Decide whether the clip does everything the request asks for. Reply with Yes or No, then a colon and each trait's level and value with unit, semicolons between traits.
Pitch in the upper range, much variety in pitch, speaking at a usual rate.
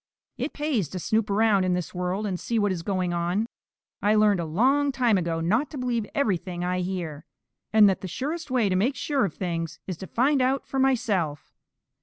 No: high, 200 Hz; wide, 5.8 semitones; fast, 210 wpm